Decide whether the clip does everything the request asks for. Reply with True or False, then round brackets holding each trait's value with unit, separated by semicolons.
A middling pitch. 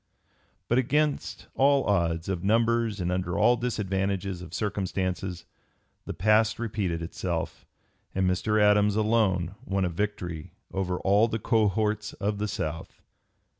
False (100 Hz)